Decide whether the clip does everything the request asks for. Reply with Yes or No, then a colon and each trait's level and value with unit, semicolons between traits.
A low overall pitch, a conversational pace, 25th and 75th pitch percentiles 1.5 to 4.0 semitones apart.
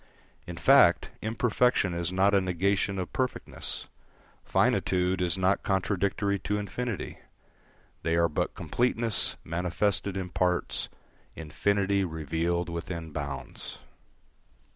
No: very low, 95 Hz; slow, 105 wpm; average, 2.9 semitones